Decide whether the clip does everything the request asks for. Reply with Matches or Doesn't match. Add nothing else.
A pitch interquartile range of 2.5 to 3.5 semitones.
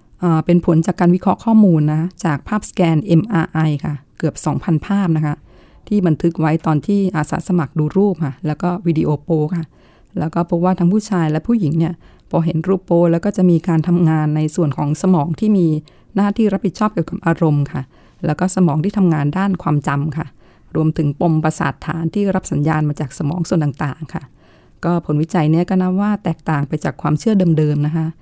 Matches